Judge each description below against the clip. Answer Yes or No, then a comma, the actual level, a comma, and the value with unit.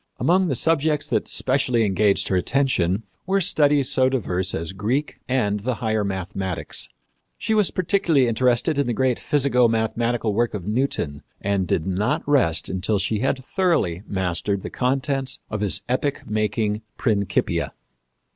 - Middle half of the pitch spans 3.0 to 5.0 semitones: No, wide, 5.5 semitones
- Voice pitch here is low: Yes, low, 115 Hz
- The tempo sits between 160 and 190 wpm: No, average, 150 wpm